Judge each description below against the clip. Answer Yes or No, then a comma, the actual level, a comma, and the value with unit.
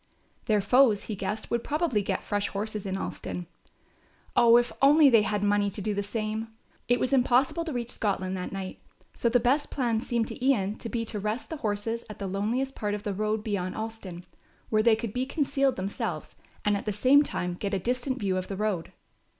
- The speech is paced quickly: Yes, fast, 215 wpm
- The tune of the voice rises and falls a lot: No, average, 3.4 semitones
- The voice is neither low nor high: No, high, 215 Hz